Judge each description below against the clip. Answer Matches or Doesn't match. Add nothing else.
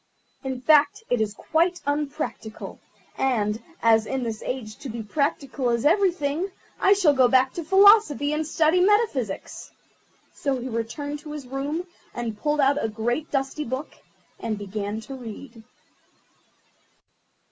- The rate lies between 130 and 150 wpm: Matches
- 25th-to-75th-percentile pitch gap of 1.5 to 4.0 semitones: Doesn't match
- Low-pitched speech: Doesn't match